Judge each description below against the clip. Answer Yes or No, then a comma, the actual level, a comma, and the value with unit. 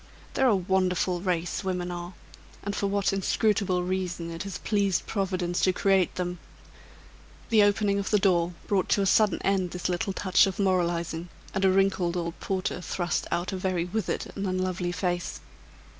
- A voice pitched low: No, medium, 185 Hz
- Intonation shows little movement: Yes, narrow, 1.8 semitones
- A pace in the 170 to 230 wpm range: Yes, average, 175 wpm